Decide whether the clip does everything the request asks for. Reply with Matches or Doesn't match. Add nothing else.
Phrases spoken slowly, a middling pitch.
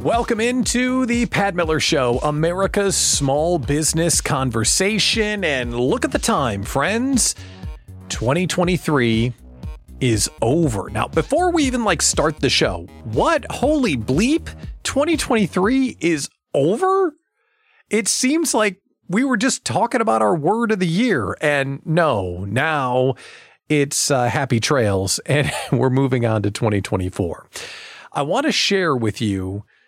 Matches